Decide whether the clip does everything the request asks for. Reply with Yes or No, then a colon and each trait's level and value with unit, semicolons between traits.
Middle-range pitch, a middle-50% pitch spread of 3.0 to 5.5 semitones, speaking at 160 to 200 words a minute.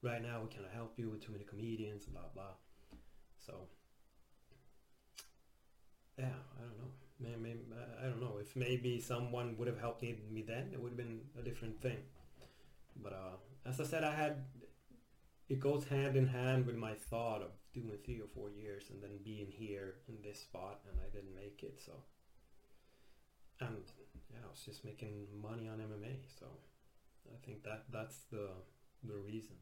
No: low, 115 Hz; average, 3.6 semitones; average, 180 wpm